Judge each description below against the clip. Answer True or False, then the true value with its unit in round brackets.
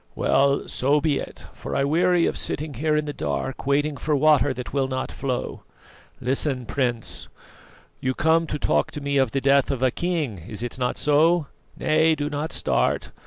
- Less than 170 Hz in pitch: True (140 Hz)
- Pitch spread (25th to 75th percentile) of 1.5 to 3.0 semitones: True (2.7 semitones)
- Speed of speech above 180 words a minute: True (190 wpm)